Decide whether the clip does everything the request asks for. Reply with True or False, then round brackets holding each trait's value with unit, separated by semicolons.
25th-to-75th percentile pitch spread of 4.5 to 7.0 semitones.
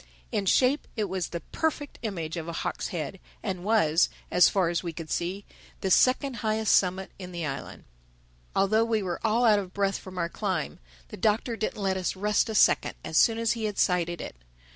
False (3.8 semitones)